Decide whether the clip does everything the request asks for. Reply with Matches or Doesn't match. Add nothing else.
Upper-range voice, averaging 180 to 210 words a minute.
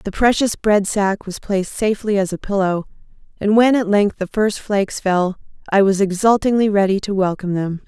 Matches